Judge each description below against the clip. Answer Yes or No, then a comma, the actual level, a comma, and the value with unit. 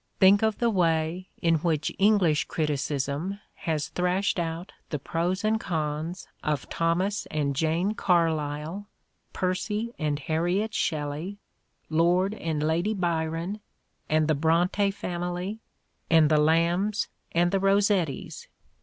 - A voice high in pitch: No, medium, 170 Hz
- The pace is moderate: No, slow, 120 wpm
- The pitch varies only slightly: No, average, 3.8 semitones